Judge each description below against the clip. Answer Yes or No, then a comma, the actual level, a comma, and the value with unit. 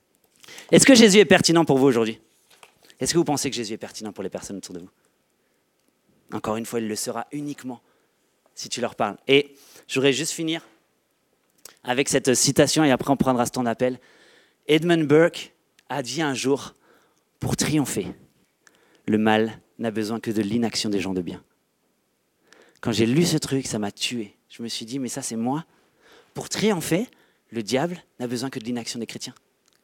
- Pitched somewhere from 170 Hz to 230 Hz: No, low, 125 Hz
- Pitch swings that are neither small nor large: Yes, average, 4.5 semitones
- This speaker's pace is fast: No, average, 185 wpm